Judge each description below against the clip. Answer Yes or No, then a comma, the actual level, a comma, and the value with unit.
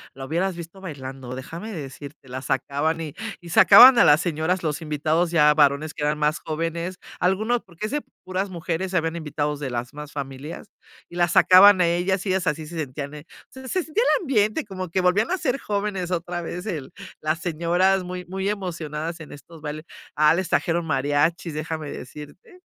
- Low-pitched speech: No, medium, 165 Hz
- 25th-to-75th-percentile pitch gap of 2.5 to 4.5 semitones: Yes, average, 3.8 semitones